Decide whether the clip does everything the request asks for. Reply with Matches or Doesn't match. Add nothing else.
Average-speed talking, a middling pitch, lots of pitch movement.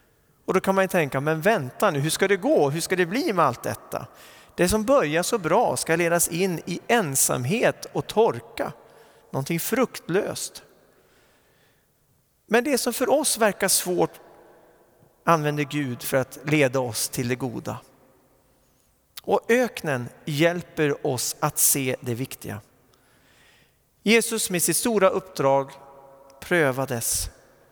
Matches